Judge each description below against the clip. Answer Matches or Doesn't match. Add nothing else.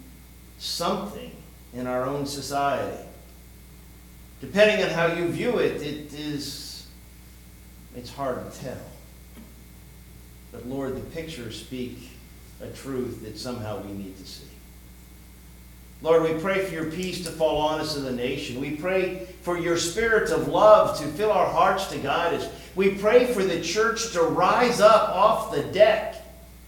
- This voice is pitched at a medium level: Doesn't match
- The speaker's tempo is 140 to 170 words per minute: Matches